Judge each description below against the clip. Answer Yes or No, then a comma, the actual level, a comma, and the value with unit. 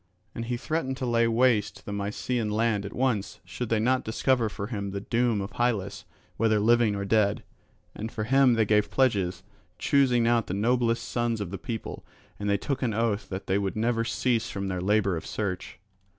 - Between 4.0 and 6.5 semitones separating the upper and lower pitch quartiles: No, average, 3.0 semitones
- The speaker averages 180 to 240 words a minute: Yes, average, 195 wpm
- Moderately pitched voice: No, low, 110 Hz